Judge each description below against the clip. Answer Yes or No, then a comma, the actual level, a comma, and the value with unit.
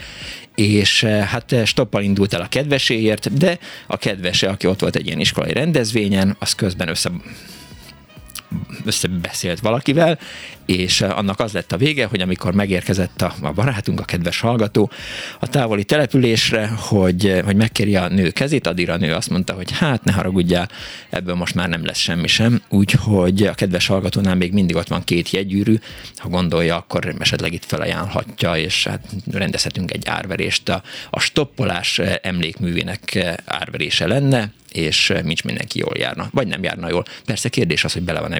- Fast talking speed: Yes, fast, 160 wpm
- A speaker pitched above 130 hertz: No, low, 100 Hz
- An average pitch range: Yes, average, 3.8 semitones